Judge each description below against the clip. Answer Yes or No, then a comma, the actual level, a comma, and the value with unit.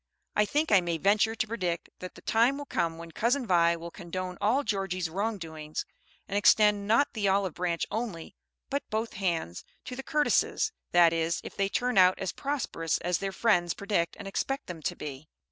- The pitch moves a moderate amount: Yes, average, 4.7 semitones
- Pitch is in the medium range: No, high, 195 Hz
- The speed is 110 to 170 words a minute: No, average, 195 wpm